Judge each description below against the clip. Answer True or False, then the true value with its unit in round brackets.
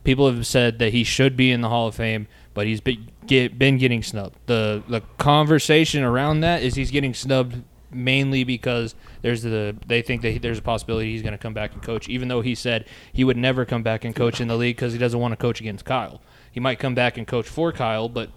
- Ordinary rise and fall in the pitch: False (2.3 semitones)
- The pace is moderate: False (250 wpm)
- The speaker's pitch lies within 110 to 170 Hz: True (120 Hz)